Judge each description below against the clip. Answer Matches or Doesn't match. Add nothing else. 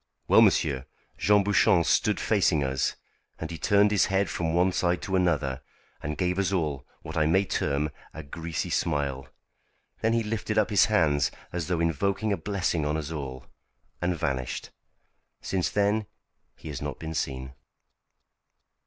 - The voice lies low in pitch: Matches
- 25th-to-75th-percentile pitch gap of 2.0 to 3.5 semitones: Doesn't match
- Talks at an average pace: Matches